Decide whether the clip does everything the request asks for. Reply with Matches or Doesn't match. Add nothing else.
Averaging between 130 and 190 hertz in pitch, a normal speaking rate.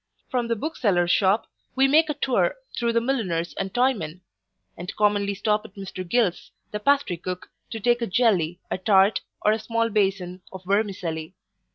Doesn't match